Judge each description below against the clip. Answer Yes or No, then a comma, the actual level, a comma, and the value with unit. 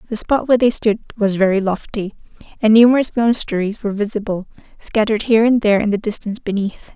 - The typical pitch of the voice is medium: No, high, 215 Hz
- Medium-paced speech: Yes, average, 180 wpm